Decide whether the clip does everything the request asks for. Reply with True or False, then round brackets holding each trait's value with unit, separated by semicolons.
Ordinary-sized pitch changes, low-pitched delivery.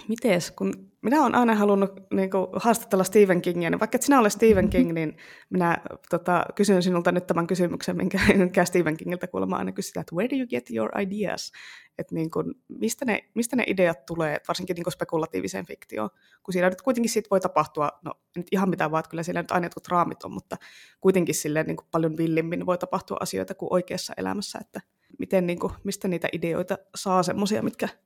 False (3.2 semitones; 180 Hz)